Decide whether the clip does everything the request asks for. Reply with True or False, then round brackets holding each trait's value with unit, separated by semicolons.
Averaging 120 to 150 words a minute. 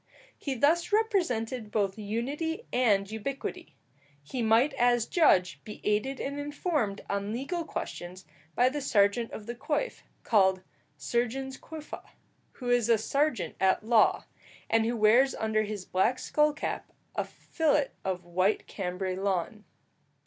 True (140 wpm)